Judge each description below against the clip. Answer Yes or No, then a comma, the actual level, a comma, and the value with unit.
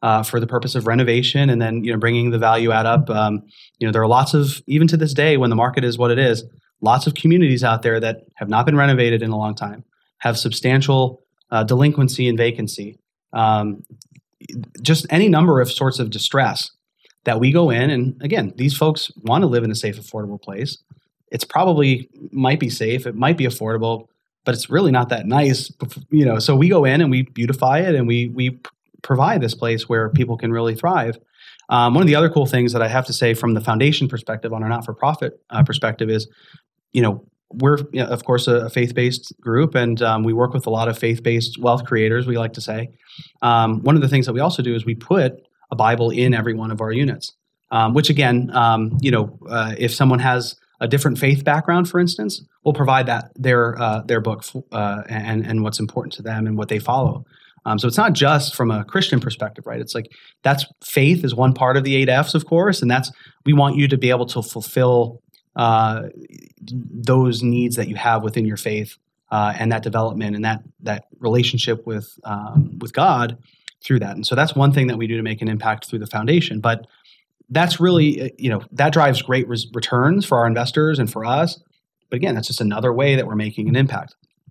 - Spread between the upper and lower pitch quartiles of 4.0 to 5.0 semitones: No, average, 3.6 semitones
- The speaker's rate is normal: No, fast, 225 wpm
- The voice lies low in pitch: Yes, low, 125 Hz